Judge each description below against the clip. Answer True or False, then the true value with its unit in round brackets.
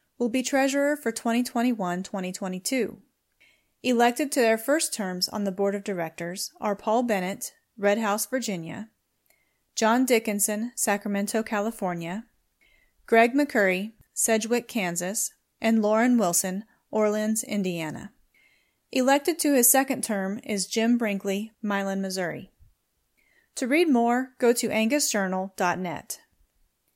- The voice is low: False (220 Hz)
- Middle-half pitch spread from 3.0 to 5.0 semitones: True (3.5 semitones)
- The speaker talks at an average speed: False (115 wpm)